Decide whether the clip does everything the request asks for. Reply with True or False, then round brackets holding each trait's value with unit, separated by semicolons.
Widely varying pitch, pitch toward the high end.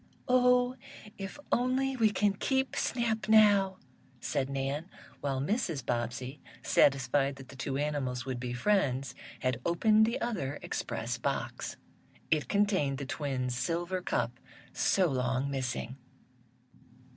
False (8.1 semitones; 145 Hz)